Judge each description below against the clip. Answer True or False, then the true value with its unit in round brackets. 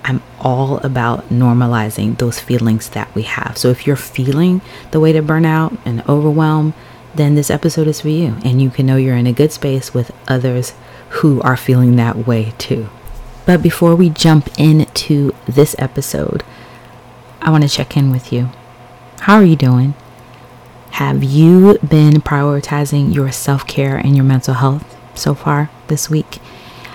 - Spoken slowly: False (170 wpm)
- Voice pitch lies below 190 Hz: True (135 Hz)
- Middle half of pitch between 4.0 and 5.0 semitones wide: False (3.6 semitones)